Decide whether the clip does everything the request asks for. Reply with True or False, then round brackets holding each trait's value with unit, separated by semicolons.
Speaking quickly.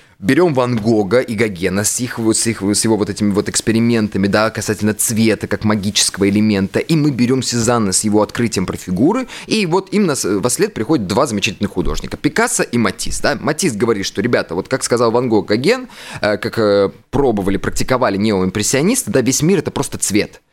True (185 wpm)